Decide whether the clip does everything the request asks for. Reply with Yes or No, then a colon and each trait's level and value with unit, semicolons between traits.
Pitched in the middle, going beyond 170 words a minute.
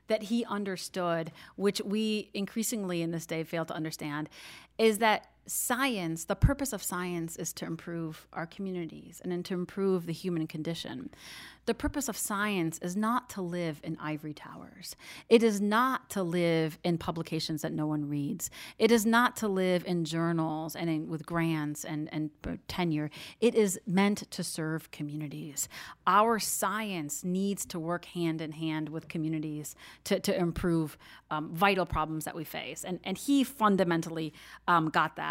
No: medium, 175 Hz; average, 165 wpm